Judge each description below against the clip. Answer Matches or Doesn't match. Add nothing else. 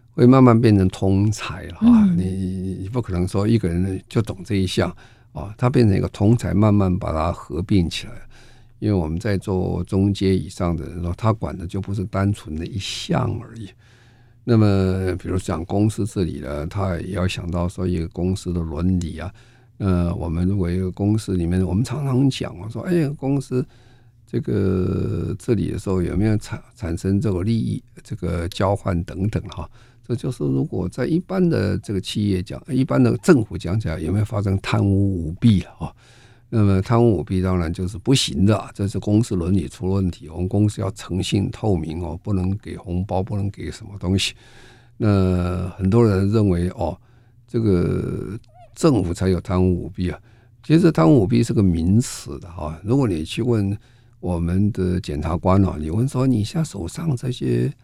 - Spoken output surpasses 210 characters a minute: Matches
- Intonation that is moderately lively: Matches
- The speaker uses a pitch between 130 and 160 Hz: Doesn't match